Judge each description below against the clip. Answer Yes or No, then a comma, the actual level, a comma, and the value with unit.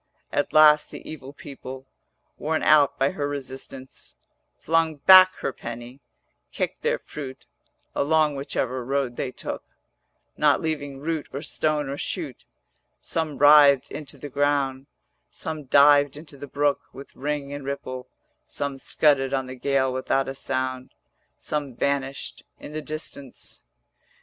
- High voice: No, medium, 140 Hz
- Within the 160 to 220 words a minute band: No, average, 140 wpm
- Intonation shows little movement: Yes, narrow, 2.0 semitones